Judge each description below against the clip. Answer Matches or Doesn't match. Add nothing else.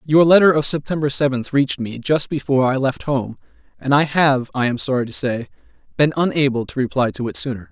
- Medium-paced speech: Doesn't match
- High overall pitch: Doesn't match